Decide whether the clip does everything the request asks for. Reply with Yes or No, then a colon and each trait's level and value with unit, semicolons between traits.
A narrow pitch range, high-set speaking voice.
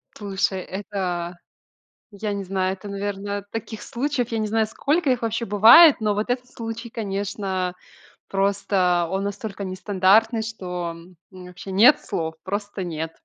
No: average, 3.0 semitones; high, 200 Hz